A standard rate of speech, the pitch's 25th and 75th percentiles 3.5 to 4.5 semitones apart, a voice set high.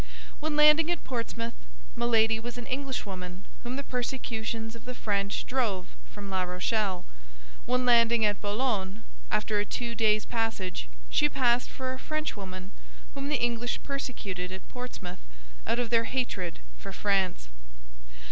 Yes: average, 145 wpm; average, 4.1 semitones; high, 230 Hz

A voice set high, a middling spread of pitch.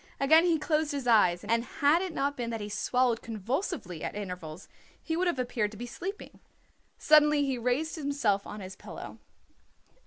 No: very high, 250 Hz; wide, 6.4 semitones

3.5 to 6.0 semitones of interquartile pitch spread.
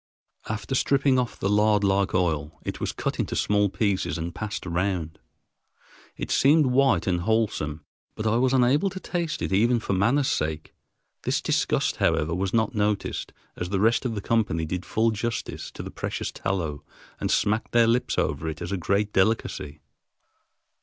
Yes: average, 4.6 semitones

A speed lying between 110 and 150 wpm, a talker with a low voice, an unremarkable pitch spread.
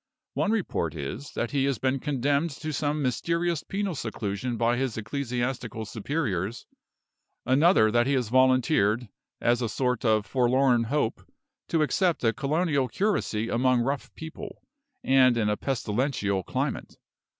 Yes: average, 140 wpm; low, 130 Hz; average, 4.0 semitones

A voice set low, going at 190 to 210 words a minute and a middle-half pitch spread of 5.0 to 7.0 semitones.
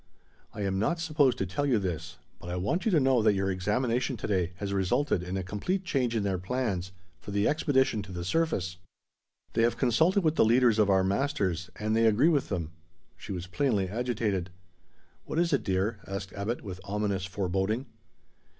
Yes: low, 105 Hz; average, 195 wpm; wide, 5.4 semitones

